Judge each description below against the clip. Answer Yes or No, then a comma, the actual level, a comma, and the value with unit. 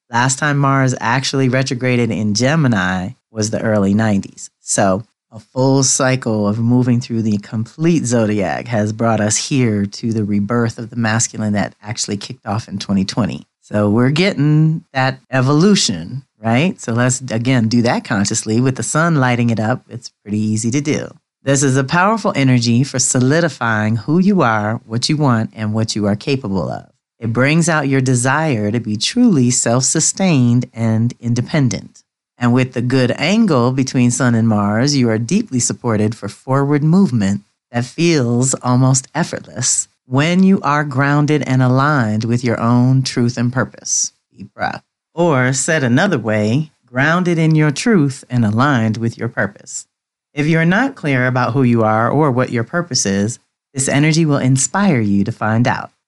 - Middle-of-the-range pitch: No, low, 125 Hz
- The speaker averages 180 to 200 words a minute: No, average, 170 wpm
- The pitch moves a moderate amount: Yes, average, 3.8 semitones